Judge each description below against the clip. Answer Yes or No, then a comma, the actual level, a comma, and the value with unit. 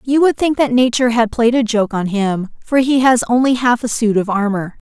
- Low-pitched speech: No, high, 235 Hz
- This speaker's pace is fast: Yes, fast, 245 wpm